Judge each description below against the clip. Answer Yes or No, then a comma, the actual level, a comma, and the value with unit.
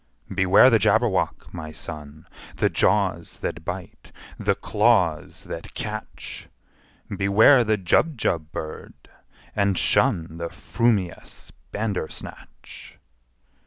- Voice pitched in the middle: No, very low, 95 Hz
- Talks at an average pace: No, slow, 95 wpm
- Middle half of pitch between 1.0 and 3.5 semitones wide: No, average, 4.5 semitones